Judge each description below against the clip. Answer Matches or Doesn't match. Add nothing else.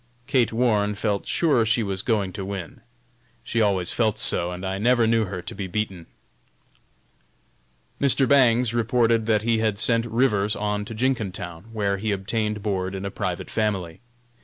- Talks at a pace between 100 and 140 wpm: Doesn't match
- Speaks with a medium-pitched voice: Doesn't match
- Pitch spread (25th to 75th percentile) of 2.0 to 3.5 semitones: Matches